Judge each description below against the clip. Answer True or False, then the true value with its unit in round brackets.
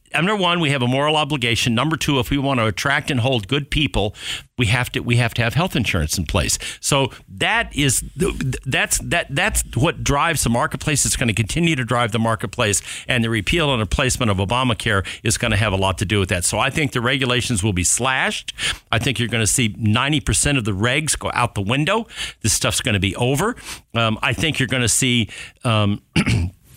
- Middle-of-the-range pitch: False (120 Hz)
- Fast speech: True (230 wpm)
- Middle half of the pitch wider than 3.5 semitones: True (4.2 semitones)